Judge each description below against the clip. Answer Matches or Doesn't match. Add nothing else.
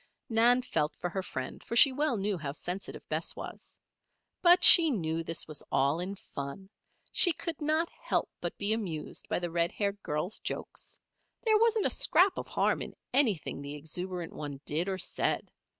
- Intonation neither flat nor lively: Doesn't match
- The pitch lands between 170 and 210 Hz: Matches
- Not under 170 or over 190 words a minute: Matches